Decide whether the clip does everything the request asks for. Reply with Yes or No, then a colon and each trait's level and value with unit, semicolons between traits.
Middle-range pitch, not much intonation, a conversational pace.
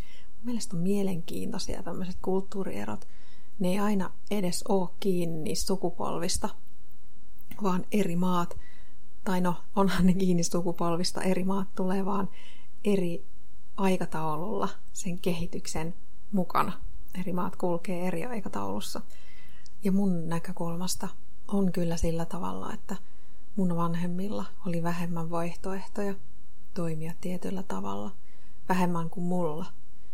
Yes: medium, 180 Hz; narrow, 2.0 semitones; average, 110 wpm